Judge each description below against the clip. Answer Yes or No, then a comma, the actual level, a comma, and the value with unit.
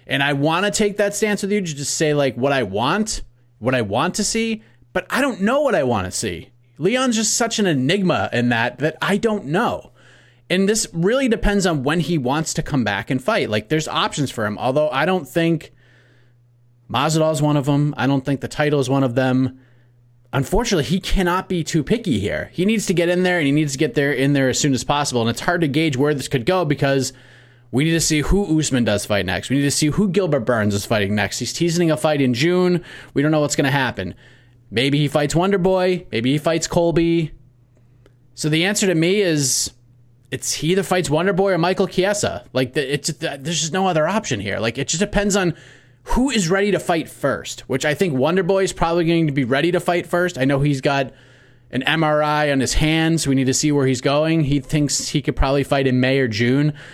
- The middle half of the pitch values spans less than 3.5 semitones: No, wide, 5.5 semitones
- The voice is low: No, medium, 150 Hz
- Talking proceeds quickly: Yes, fast, 240 wpm